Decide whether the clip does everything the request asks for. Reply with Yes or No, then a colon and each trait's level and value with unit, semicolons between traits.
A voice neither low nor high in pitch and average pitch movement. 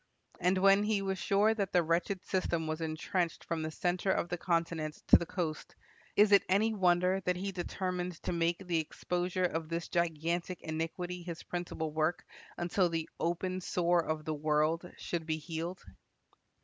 No: medium, 175 Hz; narrow, 2.1 semitones